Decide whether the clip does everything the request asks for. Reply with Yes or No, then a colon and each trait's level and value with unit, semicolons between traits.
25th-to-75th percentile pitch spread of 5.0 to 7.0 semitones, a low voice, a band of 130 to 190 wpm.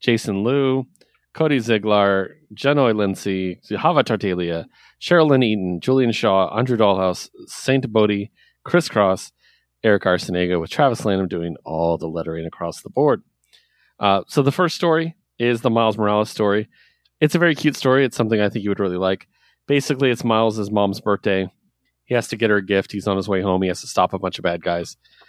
Yes: wide, 5.5 semitones; low, 105 Hz; average, 185 wpm